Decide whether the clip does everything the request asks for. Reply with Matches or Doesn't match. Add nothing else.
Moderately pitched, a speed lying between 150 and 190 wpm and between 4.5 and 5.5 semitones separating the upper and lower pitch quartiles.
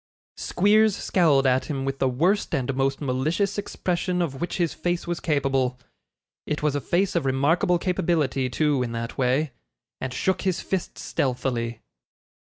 Matches